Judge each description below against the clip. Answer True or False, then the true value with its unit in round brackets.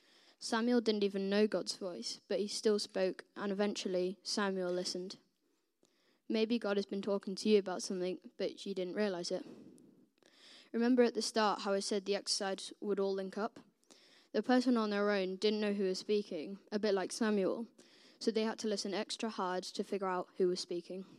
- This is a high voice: True (205 Hz)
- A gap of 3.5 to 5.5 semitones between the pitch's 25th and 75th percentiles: False (2.9 semitones)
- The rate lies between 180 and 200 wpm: True (195 wpm)